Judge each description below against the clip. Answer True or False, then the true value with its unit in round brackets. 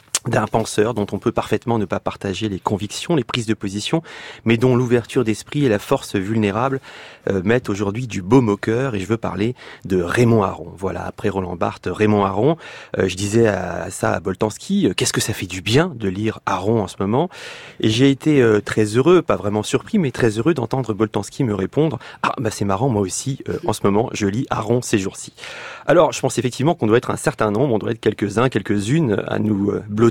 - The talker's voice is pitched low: True (110 Hz)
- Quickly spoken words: True (225 wpm)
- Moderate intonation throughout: True (3.9 semitones)